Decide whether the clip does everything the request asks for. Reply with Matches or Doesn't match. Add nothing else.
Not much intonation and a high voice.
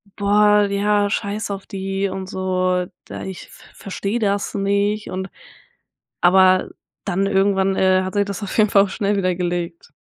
Matches